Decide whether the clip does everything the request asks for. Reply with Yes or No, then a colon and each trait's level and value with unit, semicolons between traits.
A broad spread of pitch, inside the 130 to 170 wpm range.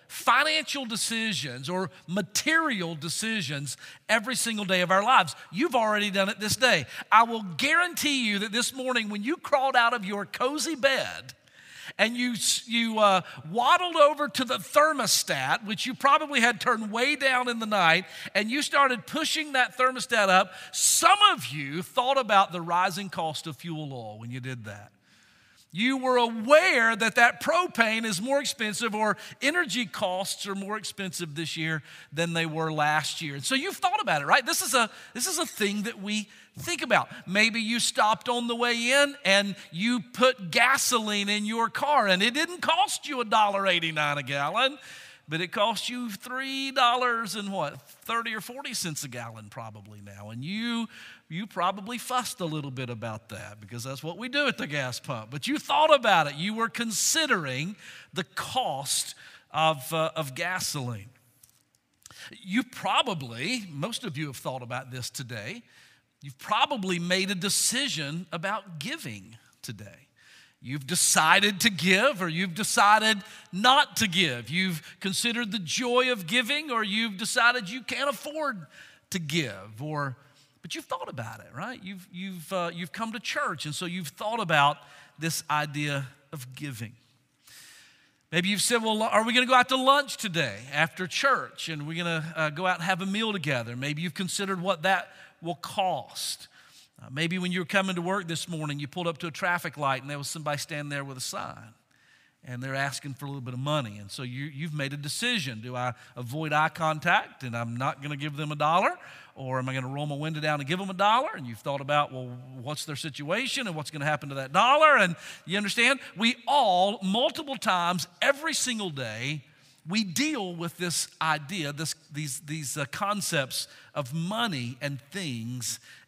No: wide, 8.0 semitones; average, 185 wpm